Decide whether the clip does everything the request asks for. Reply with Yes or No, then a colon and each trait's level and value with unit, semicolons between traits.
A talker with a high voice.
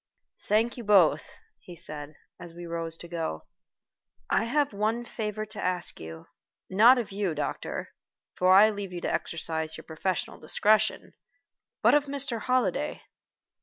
Yes: high, 195 Hz